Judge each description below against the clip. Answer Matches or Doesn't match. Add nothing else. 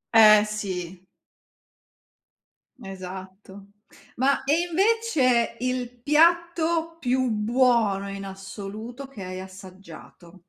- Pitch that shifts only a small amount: Doesn't match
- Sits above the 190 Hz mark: Matches